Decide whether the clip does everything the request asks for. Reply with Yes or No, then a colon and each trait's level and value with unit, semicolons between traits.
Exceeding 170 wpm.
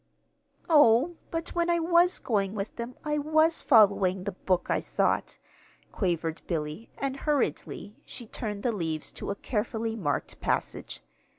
No: average, 150 wpm